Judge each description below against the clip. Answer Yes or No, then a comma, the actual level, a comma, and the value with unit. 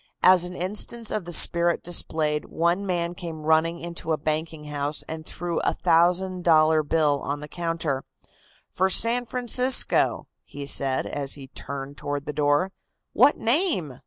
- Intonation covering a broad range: No, average, 3.3 semitones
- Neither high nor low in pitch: Yes, medium, 165 Hz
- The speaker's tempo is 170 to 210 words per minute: No, average, 160 wpm